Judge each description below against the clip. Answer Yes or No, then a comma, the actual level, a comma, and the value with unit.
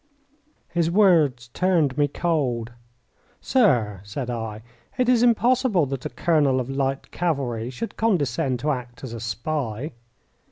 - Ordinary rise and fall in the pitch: No, wide, 6.1 semitones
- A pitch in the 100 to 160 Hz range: Yes, medium, 140 Hz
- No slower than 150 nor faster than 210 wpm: No, slow, 135 wpm